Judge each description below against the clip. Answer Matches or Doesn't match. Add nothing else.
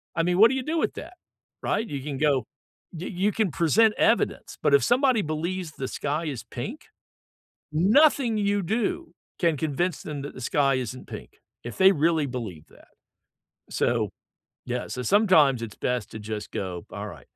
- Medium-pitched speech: Matches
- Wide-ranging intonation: Matches